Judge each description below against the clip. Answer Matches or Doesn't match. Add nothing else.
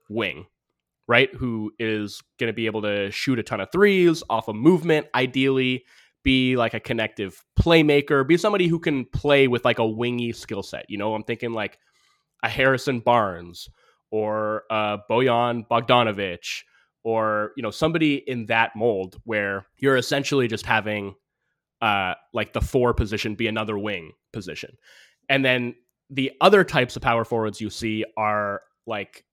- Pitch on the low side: Matches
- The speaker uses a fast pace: Doesn't match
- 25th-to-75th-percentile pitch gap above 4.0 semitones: Doesn't match